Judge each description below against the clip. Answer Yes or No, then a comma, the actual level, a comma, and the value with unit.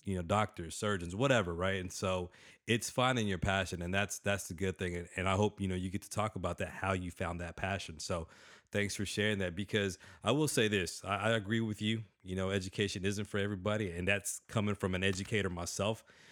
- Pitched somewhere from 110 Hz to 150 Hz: No, low, 100 Hz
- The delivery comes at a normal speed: No, fast, 230 wpm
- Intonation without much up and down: Yes, narrow, 2.2 semitones